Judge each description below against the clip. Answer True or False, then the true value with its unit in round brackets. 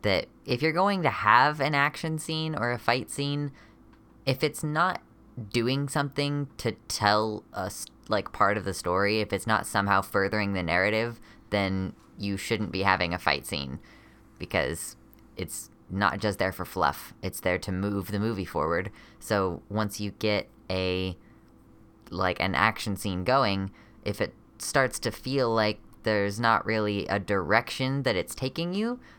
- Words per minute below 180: True (165 wpm)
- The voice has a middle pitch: False (110 Hz)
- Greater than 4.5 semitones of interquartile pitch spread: True (5.2 semitones)